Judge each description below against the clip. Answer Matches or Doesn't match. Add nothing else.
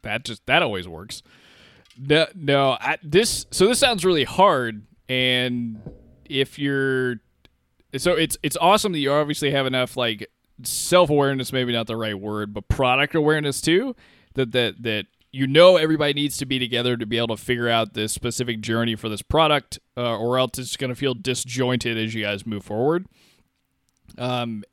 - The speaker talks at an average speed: Matches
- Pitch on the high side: Doesn't match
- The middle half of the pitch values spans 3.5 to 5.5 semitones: Matches